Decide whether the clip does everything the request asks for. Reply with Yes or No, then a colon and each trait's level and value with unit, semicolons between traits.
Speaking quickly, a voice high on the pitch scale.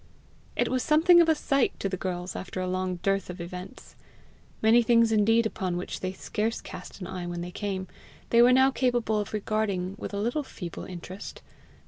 No: average, 195 wpm; high, 205 Hz